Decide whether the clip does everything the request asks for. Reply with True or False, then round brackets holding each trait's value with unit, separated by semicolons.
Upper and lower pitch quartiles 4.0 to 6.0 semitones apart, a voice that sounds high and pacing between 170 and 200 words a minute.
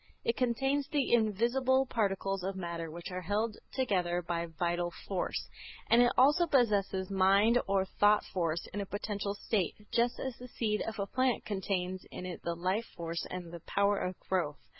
True (4.5 semitones; 200 Hz; 180 wpm)